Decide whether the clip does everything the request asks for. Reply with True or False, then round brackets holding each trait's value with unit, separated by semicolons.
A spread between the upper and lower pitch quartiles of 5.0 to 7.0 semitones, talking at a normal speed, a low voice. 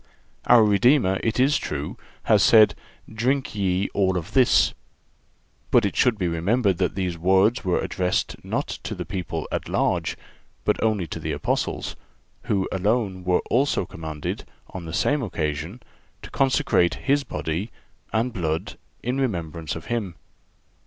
True (5.4 semitones; 150 wpm; 95 Hz)